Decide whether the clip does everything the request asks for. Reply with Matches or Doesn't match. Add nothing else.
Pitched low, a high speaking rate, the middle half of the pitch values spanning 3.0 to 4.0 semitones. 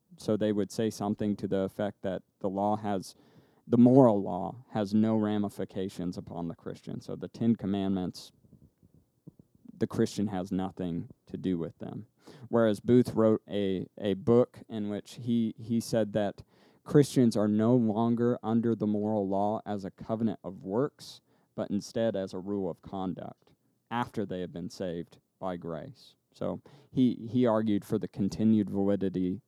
Doesn't match